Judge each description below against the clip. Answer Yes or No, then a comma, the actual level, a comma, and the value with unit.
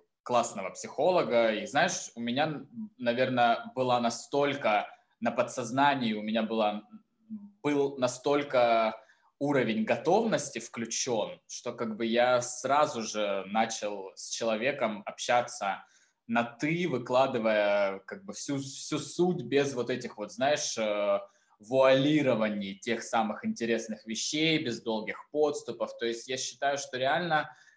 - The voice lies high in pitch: No, low, 125 Hz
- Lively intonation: No, average, 4.2 semitones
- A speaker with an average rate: Yes, average, 125 wpm